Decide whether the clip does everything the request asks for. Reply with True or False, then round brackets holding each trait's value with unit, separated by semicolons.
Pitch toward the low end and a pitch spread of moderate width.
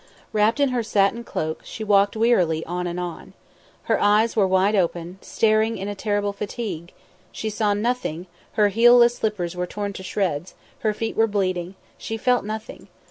False (205 Hz; 3.3 semitones)